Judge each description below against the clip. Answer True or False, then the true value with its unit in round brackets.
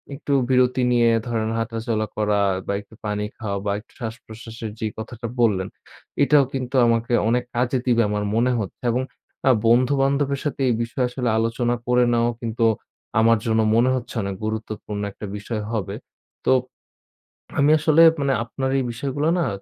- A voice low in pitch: True (115 Hz)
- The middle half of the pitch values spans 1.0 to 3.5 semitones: True (2.5 semitones)